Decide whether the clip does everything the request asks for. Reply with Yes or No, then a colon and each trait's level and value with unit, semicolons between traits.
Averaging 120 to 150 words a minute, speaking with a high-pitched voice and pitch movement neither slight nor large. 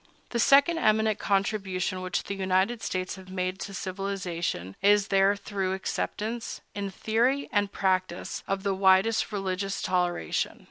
No: average, 140 wpm; high, 195 Hz; narrow, 1.9 semitones